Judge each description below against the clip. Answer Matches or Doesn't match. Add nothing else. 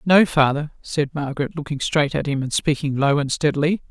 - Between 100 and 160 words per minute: Doesn't match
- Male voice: Doesn't match